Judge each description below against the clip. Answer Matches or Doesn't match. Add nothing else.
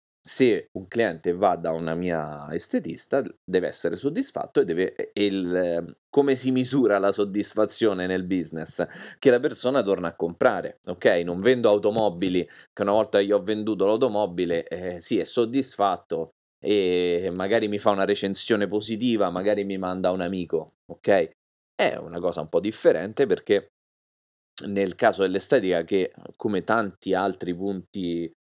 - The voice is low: Matches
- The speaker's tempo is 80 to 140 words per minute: Doesn't match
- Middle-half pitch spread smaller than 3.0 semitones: Doesn't match